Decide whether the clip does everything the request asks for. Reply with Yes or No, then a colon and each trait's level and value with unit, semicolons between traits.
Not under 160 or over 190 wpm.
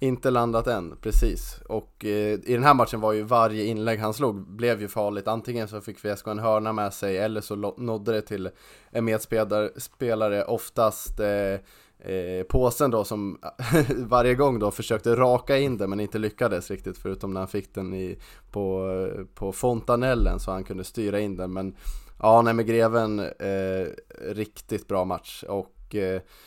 Yes: average, 180 wpm